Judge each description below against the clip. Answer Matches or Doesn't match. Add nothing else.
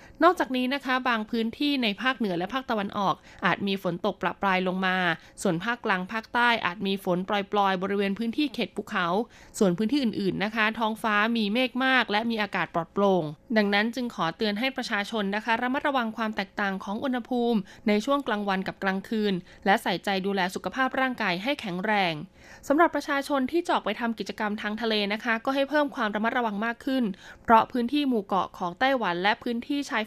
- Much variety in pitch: Doesn't match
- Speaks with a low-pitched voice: Doesn't match